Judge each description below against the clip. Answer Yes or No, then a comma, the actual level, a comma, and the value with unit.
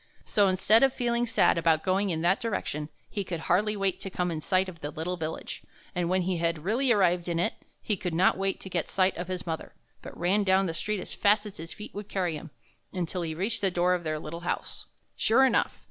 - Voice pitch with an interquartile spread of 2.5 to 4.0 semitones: Yes, average, 3.2 semitones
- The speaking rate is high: Yes, fast, 245 wpm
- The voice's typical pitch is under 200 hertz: Yes, medium, 185 Hz